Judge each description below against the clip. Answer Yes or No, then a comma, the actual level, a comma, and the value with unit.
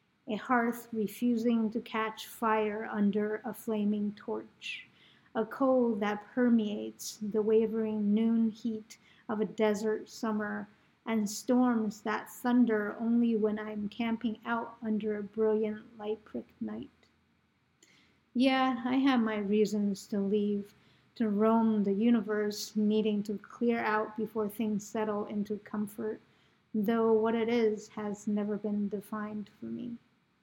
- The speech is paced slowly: Yes, slow, 130 wpm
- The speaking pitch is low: No, high, 215 Hz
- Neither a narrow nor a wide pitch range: No, narrow, 1.5 semitones